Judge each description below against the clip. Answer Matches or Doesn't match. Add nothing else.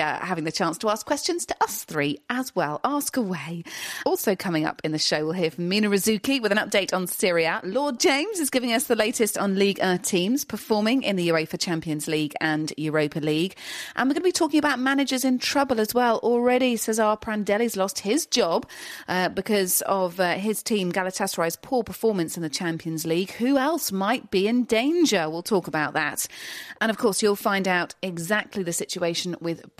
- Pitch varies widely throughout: Matches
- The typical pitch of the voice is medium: Doesn't match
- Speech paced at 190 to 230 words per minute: Matches